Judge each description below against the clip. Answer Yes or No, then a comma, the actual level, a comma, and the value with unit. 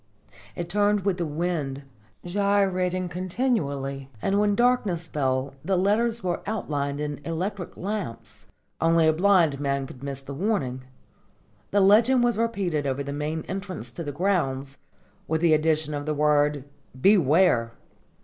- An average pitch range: No, wide, 5.8 semitones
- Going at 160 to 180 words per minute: No, average, 145 wpm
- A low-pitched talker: No, medium, 165 Hz